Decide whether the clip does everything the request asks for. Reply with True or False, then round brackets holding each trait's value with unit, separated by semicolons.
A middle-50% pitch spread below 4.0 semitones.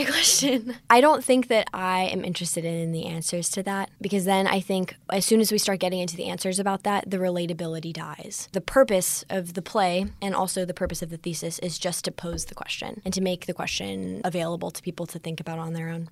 True (2.4 semitones)